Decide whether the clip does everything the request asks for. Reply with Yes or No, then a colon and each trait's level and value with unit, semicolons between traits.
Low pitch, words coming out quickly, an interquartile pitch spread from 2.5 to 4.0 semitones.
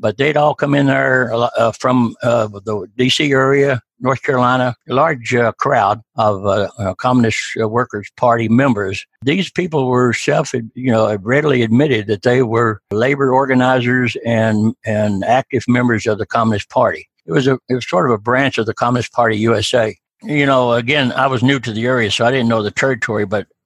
No: low, 120 Hz; average, 195 wpm; average, 2.8 semitones